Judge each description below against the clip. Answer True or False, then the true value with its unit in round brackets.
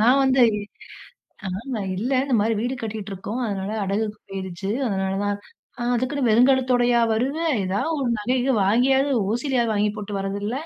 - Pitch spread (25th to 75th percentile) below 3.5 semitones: False (4.0 semitones)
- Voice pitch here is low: False (225 Hz)